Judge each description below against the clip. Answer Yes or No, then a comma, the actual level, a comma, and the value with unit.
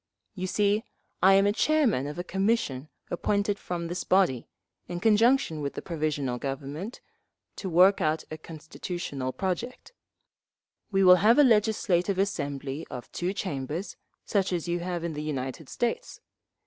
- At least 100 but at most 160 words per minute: Yes, average, 150 wpm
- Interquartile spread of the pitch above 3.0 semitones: Yes, average, 5.0 semitones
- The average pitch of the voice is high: No, medium, 180 Hz